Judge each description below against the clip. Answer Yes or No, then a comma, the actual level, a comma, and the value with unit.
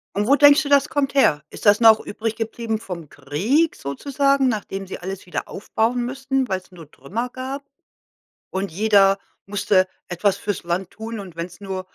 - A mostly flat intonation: No, wide, 5.6 semitones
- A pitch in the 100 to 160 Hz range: No, high, 210 Hz